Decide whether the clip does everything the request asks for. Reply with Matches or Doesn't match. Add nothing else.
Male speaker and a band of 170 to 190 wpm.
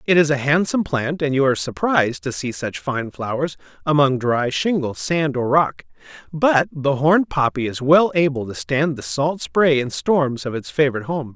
Doesn't match